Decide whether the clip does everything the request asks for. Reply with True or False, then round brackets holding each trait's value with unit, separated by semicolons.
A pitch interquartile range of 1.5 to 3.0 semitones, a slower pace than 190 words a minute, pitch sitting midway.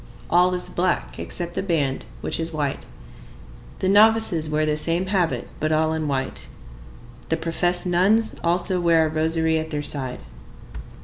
True (2.5 semitones; 160 wpm; 165 Hz)